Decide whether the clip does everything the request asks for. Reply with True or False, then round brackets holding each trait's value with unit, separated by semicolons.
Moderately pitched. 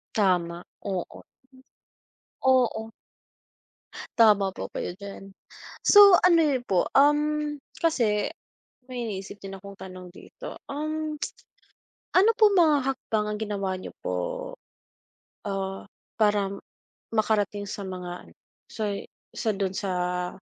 False (210 Hz)